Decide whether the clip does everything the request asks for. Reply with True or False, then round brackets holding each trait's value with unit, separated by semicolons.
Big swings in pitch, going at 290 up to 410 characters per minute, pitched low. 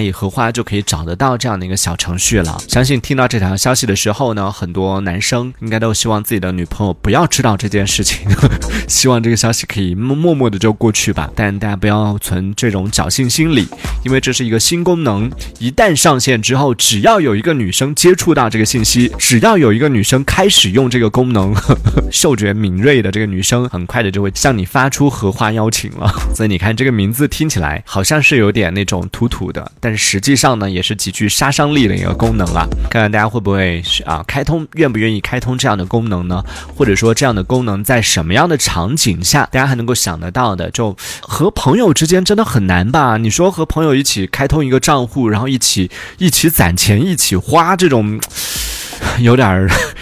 False (5.0 semitones; 330 characters per minute; 110 Hz)